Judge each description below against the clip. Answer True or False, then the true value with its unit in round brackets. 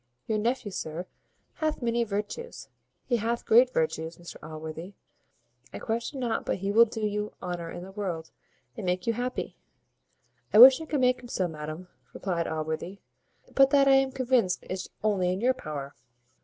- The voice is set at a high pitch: True (210 Hz)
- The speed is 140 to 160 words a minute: False (175 wpm)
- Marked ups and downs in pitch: True (5.9 semitones)